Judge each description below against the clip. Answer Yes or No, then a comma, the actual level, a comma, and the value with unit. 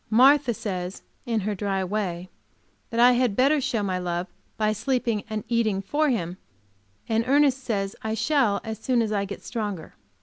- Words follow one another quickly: No, average, 175 wpm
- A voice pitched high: Yes, high, 220 Hz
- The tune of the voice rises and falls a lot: No, average, 3.9 semitones